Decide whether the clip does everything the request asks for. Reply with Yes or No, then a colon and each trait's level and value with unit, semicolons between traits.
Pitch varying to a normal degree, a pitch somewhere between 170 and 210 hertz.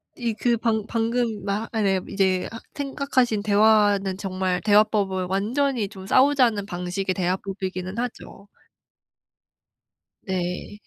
Yes: average, 3.2 semitones; high, 205 Hz